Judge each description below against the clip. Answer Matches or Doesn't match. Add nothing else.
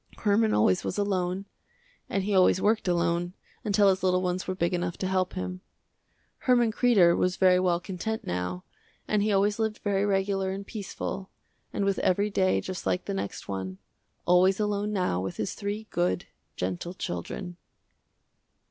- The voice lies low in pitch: Doesn't match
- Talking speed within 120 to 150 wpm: Doesn't match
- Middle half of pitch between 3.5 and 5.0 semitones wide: Doesn't match